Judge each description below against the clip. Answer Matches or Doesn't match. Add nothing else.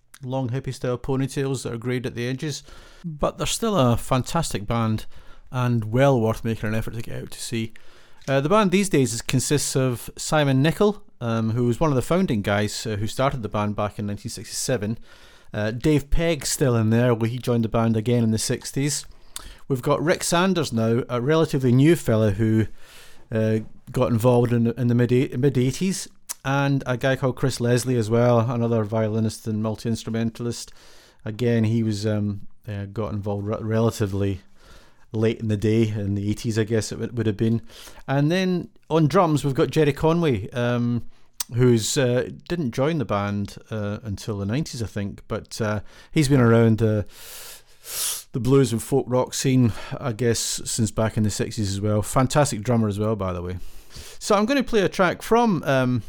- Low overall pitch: Matches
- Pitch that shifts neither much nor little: Matches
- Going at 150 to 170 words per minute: Doesn't match